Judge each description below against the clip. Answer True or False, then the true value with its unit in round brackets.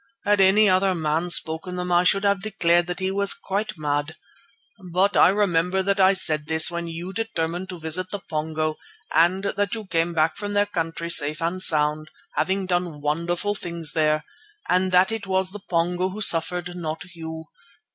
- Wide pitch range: False (2.9 semitones)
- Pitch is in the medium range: True (175 Hz)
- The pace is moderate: True (185 wpm)